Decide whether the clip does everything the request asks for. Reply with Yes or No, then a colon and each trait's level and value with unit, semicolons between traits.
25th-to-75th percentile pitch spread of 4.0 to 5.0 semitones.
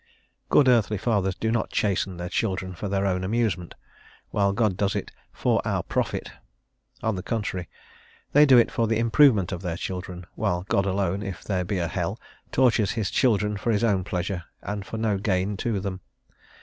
No: average, 3.1 semitones